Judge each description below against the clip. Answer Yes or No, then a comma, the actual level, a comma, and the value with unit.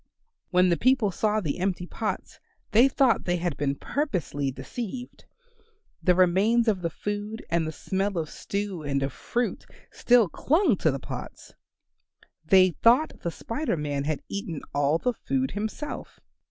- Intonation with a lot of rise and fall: Yes, wide, 6.2 semitones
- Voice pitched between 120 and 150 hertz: No, high, 190 Hz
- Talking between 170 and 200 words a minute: No, average, 155 wpm